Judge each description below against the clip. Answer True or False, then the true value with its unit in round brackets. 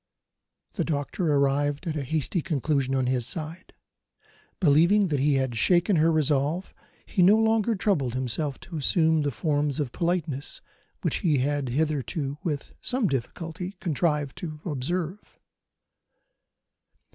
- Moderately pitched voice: True (150 Hz)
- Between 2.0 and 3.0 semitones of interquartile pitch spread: False (3.8 semitones)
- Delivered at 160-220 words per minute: False (135 wpm)